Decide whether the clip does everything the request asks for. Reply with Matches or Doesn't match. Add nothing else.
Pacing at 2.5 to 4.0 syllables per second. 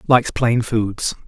Matches